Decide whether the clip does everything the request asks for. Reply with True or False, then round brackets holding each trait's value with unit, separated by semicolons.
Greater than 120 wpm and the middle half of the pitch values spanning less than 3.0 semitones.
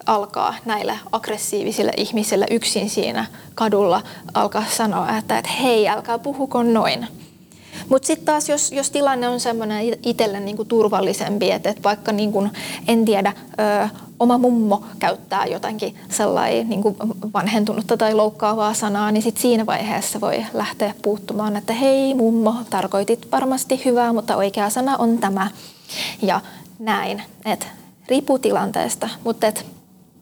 True (135 wpm; 2.4 semitones)